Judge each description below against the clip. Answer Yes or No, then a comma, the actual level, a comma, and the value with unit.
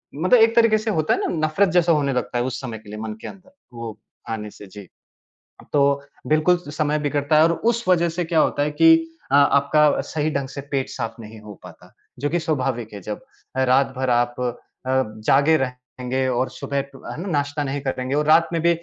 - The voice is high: No, medium, 140 Hz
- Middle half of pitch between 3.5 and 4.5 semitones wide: Yes, average, 3.9 semitones